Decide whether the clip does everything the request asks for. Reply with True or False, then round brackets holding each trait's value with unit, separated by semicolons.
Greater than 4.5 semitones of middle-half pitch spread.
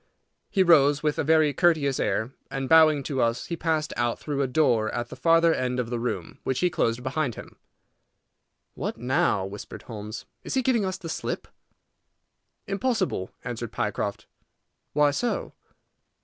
True (5.2 semitones)